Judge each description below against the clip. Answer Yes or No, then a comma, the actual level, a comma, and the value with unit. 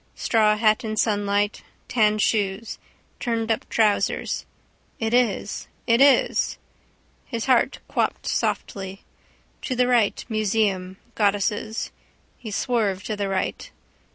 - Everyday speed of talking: No, slow, 110 wpm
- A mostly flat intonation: Yes, narrow, 2.2 semitones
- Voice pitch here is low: No, high, 215 Hz